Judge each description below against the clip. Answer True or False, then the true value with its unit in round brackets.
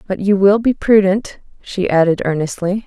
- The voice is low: False (195 Hz)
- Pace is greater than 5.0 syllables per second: False (4.8 syllables/s)